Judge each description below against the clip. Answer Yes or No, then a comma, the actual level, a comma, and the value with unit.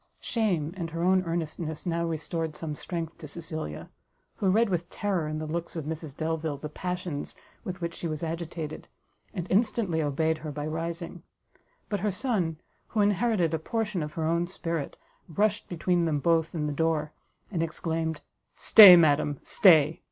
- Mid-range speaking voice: Yes, medium, 165 Hz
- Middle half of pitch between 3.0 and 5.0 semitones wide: No, narrow, 2.4 semitones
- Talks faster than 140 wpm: Yes, average, 170 wpm